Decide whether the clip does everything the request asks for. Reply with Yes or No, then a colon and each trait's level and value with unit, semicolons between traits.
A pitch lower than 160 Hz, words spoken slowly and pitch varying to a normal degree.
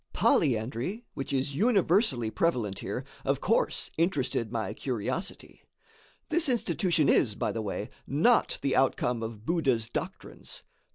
No: low, 135 Hz; slow, 125 wpm; wide, 7.6 semitones